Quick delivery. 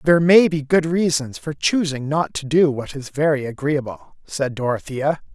No: average, 190 wpm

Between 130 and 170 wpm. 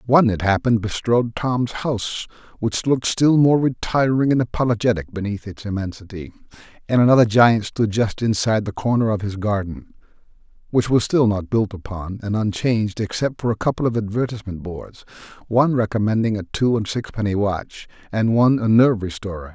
Yes: average, 165 wpm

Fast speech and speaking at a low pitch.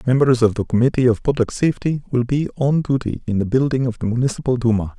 Yes: fast, 215 wpm; low, 125 Hz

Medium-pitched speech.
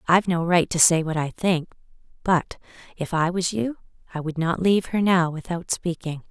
Yes: medium, 175 Hz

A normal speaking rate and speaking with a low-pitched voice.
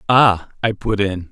Yes: average, 180 wpm; low, 105 Hz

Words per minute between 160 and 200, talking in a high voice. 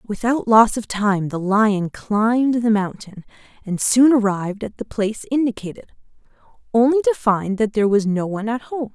Yes: average, 175 wpm; high, 220 Hz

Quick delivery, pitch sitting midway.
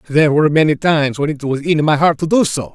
Yes: fast, 285 wpm; medium, 150 Hz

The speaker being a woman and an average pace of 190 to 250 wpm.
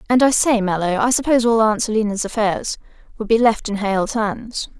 Yes: female; average, 200 wpm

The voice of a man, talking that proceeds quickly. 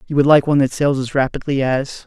Yes: male; fast, 260 wpm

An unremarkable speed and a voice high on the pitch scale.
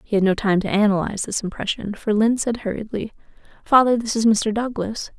Yes: average, 195 wpm; high, 215 Hz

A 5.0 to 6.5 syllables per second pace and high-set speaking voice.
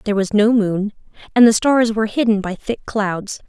Yes: 5.2 syllables/s; high, 215 Hz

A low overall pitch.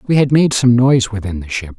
Yes: low, 120 Hz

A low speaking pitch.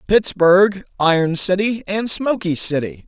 No: medium, 185 Hz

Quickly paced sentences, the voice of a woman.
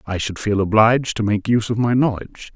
No: fast, 235 wpm; male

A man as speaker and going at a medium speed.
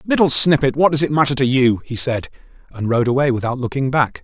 No: male; fast, 225 wpm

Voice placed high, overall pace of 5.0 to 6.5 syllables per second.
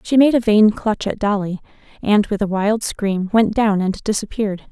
No: high, 210 Hz; 4.8 syllables/s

